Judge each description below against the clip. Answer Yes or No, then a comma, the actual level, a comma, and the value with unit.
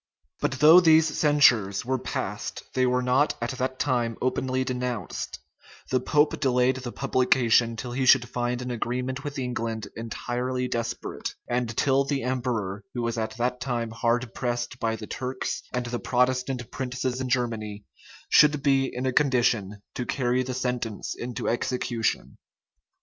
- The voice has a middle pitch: No, low, 125 Hz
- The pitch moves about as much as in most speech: No, narrow, 1.7 semitones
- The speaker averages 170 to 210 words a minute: No, average, 160 wpm